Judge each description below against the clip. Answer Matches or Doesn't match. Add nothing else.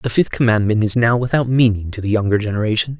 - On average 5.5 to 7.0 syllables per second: Matches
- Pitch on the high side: Doesn't match